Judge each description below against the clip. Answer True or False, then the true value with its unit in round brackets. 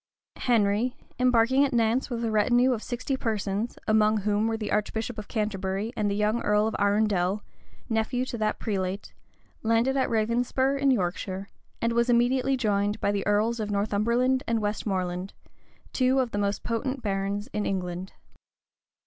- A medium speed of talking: True (160 wpm)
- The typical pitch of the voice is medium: False (220 Hz)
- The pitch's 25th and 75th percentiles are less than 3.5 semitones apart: True (3.0 semitones)